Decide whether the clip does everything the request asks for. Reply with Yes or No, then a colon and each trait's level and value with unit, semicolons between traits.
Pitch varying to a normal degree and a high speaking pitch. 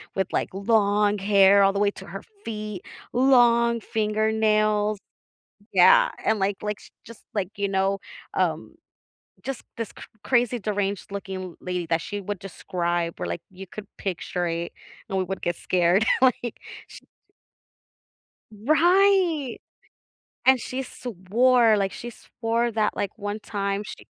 Yes: average, 3.1 semitones; high, 205 Hz